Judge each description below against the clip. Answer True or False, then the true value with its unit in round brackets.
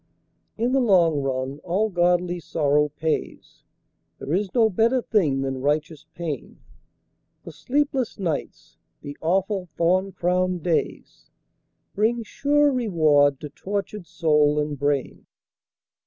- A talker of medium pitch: True (175 Hz)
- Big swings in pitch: True (5.9 semitones)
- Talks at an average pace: False (120 wpm)